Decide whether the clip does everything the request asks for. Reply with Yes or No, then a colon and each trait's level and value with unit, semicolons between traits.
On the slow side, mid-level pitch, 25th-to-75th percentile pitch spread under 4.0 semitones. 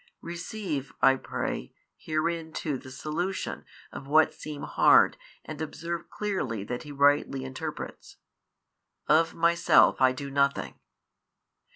Yes: slow, 115 wpm; medium, 150 Hz; average, 3.5 semitones